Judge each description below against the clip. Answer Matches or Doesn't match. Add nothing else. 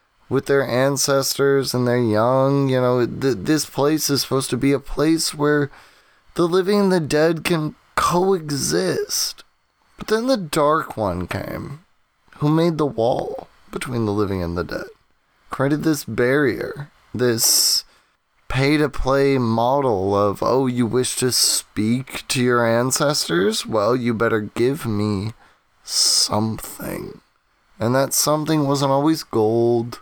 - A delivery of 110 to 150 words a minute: Matches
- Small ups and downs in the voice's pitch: Doesn't match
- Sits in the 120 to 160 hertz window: Matches